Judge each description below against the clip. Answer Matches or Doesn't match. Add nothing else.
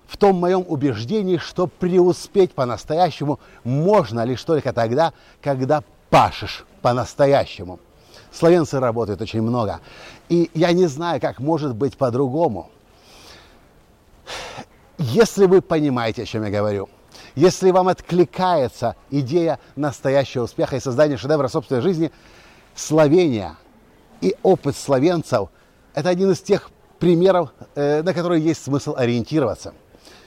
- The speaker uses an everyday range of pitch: Doesn't match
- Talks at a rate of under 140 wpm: Matches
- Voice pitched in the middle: Matches